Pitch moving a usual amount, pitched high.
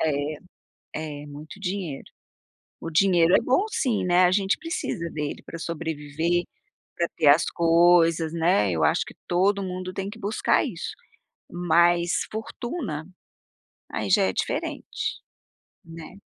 No: average, 3.0 semitones; medium, 170 Hz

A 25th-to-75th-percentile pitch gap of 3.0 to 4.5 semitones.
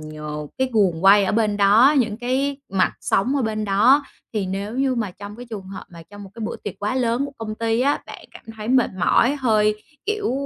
Yes: average, 4.2 semitones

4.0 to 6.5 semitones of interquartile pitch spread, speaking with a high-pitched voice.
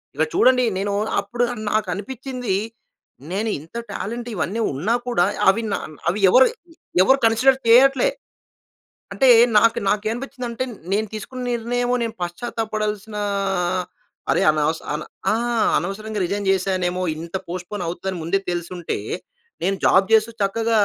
Yes: average, 4.3 semitones; high, 215 Hz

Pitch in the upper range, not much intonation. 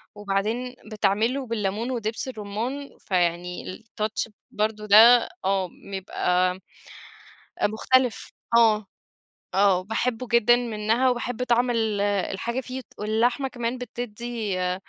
No: high, 220 Hz; average, 3.2 semitones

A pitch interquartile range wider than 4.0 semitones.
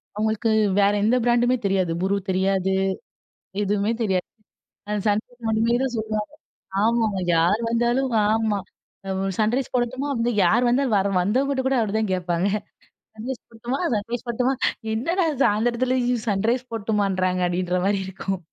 No: average, 3.7 semitones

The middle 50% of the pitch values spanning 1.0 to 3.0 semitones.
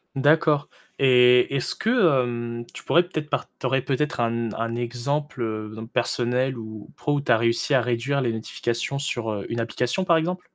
No: average, 3.4 semitones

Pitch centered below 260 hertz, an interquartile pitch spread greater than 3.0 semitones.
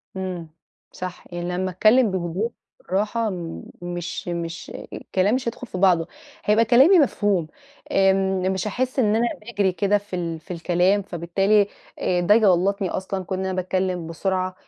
No: high, 190 Hz; average, 2.7 semitones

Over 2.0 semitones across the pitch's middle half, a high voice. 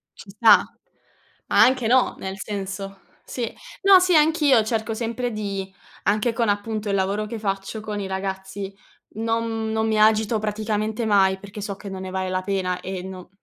Yes: narrow, 2.5 semitones; high, 210 Hz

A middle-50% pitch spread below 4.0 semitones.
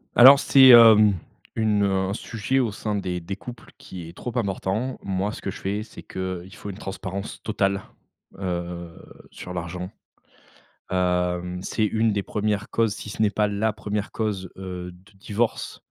Yes: average, 2.8 semitones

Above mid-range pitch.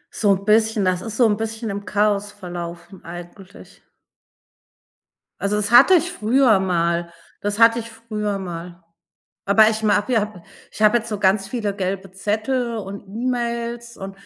Yes: high, 210 Hz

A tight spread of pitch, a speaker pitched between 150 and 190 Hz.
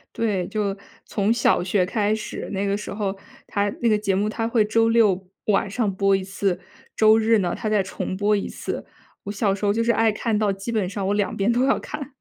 No: narrow, 2.2 semitones; high, 210 Hz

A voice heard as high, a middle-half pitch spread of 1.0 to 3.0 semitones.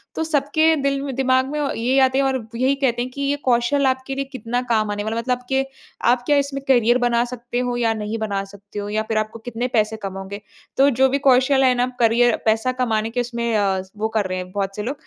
No: high, 245 Hz; average, 3.4 semitones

